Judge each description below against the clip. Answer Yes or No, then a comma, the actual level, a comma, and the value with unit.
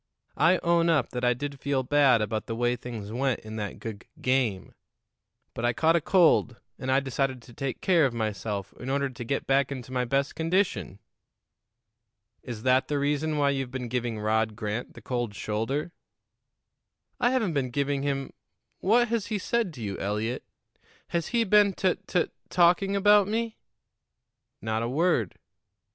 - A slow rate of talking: No, average, 175 wpm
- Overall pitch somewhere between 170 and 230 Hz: No, low, 135 Hz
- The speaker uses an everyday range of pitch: No, wide, 6.1 semitones